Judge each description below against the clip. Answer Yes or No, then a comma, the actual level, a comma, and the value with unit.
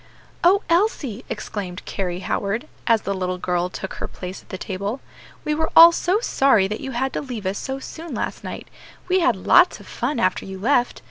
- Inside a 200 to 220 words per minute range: Yes, fast, 205 wpm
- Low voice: No, high, 230 Hz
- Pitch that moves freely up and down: Yes, wide, 7.8 semitones